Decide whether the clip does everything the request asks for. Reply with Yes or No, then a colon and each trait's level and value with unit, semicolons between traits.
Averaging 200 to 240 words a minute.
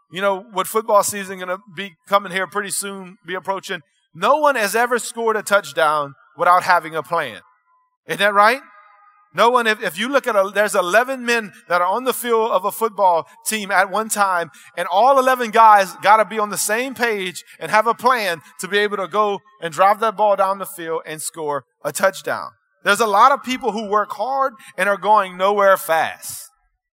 Yes: fast, 205 wpm